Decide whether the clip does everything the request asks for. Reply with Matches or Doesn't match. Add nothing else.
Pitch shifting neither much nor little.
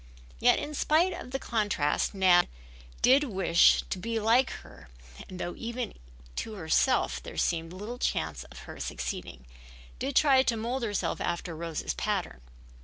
Doesn't match